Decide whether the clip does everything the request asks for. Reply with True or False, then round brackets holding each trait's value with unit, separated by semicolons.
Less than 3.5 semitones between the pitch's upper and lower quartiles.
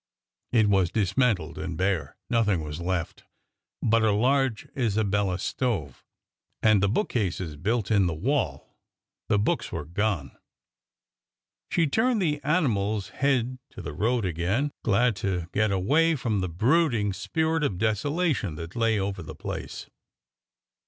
False (5.4 semitones)